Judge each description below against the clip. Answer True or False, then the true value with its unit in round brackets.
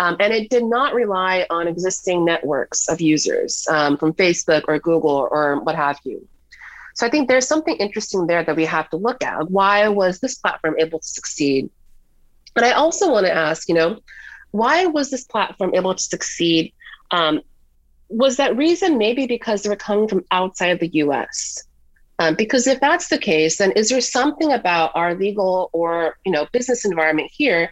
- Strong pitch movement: True (7.1 semitones)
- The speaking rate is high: False (190 wpm)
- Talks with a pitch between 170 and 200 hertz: True (185 Hz)